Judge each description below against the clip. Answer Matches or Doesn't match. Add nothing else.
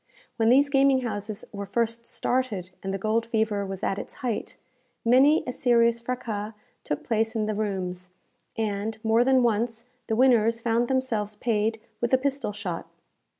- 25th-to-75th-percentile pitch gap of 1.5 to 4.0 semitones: Matches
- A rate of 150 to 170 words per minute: Matches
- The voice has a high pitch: Matches